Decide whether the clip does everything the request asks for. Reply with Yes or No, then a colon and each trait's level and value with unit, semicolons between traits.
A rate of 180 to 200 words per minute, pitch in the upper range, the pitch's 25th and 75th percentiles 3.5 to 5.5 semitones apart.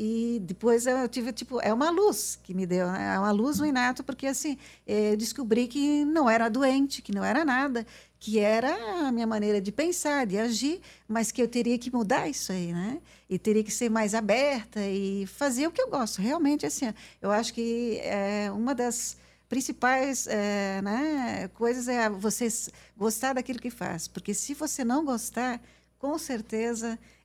Yes: fast, 185 wpm; high, 235 Hz; average, 4.0 semitones